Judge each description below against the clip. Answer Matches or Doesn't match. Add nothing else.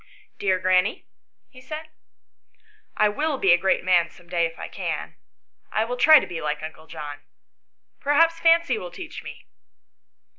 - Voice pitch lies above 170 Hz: Matches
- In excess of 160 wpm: Matches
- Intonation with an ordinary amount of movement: Doesn't match